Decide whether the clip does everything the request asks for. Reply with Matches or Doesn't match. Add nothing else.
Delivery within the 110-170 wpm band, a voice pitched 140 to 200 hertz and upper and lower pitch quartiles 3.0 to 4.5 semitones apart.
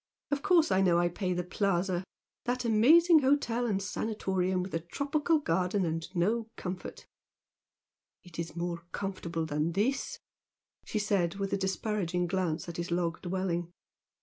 Matches